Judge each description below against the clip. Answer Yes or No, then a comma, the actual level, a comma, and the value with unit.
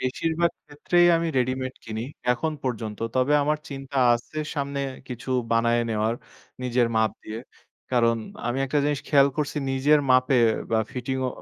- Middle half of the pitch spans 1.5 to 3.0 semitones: No, average, 3.6 semitones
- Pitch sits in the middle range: No, low, 130 Hz